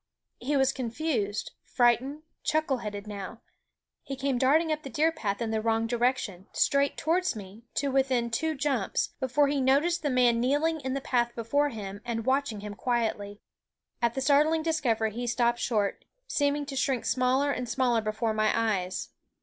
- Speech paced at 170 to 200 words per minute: Yes, average, 175 wpm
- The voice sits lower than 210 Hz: No, very high, 250 Hz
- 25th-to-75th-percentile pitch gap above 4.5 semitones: No, average, 4.0 semitones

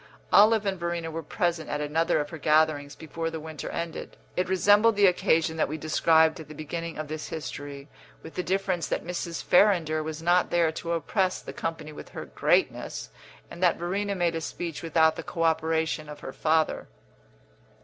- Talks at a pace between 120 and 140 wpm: No, average, 190 wpm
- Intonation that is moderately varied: No, narrow, 1.9 semitones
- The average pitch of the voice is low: No, medium, 165 Hz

